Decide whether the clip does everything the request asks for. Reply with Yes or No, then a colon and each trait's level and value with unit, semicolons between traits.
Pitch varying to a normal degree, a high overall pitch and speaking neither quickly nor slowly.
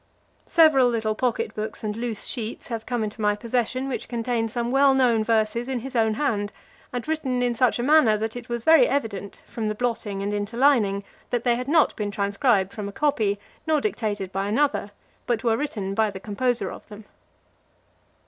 Yes: average, 3.1 semitones; high, 230 Hz; average, 195 wpm